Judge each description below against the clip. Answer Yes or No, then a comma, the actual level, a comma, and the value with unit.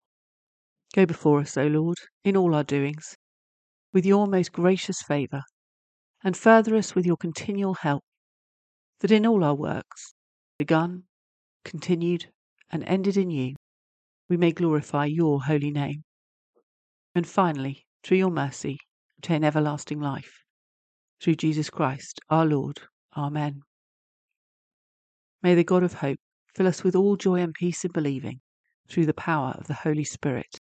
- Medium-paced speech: Yes, average, 145 wpm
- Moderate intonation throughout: Yes, average, 4.3 semitones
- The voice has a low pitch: No, medium, 155 Hz